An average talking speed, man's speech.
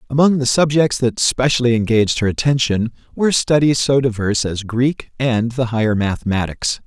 Yes: average, 155 wpm; male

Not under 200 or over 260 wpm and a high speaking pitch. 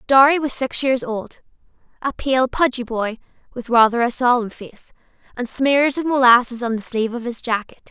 No: average, 180 wpm; high, 245 Hz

